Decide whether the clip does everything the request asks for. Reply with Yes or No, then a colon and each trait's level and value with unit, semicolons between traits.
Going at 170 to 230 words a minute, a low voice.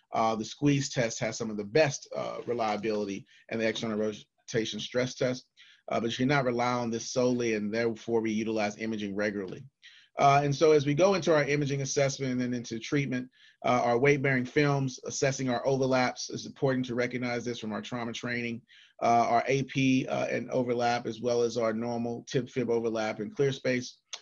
Yes: average, 200 wpm; low, 120 Hz